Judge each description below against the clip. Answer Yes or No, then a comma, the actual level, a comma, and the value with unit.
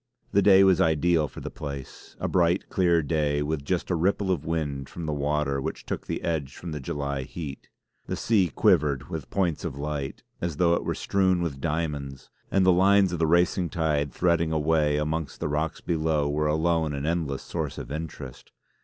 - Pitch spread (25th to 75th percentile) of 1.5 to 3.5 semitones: Yes, average, 3.0 semitones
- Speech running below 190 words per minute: No, average, 200 wpm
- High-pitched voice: No, very low, 80 Hz